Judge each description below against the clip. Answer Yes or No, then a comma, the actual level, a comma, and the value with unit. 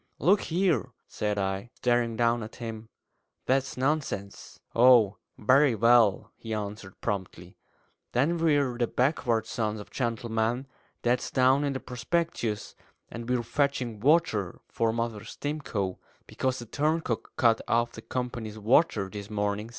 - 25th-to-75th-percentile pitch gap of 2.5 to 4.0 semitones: Yes, average, 3.5 semitones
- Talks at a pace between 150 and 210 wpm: No, slow, 135 wpm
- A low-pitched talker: Yes, low, 120 Hz